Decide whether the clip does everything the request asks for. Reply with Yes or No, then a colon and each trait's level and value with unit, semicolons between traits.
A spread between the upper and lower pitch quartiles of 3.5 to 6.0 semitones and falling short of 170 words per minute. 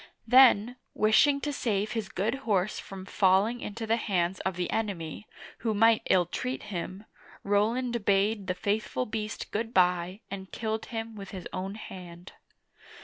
No: average, 3.0 semitones; average, 150 wpm